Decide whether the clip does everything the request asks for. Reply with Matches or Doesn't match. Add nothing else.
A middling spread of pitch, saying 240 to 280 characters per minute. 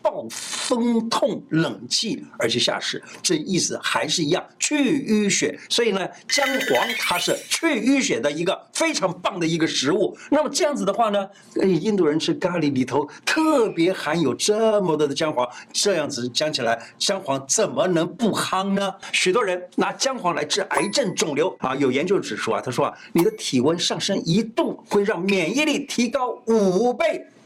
Doesn't match